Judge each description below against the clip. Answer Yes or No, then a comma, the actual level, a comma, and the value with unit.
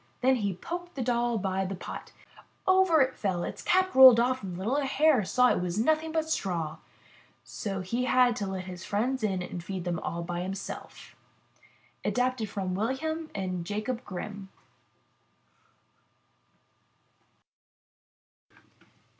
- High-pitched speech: Yes, high, 215 Hz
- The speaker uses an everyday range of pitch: No, wide, 5.7 semitones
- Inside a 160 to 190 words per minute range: No, average, 150 wpm